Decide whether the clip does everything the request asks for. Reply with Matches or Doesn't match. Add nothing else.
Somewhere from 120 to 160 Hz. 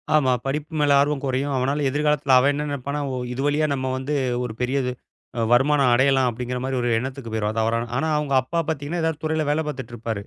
Matches